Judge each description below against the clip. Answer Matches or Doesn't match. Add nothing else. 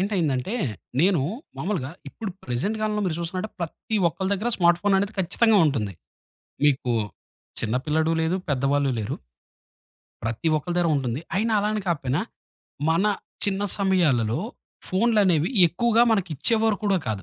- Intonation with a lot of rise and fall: Matches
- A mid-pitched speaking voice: Matches